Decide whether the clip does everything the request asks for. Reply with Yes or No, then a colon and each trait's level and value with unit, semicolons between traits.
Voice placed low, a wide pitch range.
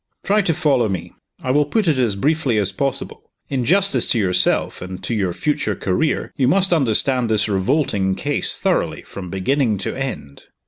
Yes: low, 125 Hz; wide, 7.1 semitones